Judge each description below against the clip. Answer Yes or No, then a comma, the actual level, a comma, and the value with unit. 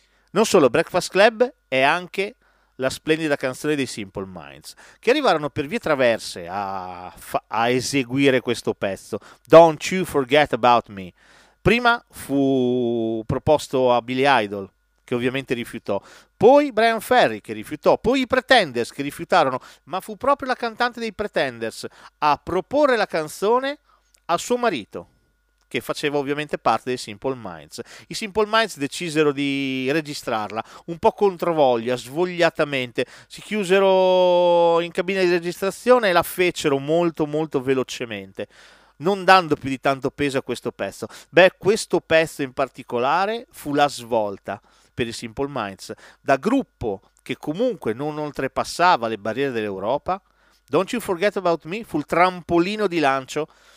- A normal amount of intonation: No, wide, 6.6 semitones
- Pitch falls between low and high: Yes, medium, 150 Hz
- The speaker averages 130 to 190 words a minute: Yes, average, 145 wpm